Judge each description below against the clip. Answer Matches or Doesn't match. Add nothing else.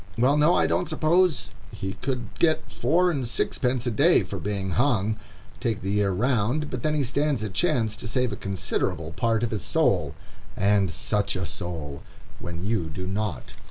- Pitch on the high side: Doesn't match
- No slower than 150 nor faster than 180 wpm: Matches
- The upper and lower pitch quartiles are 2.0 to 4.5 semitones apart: Doesn't match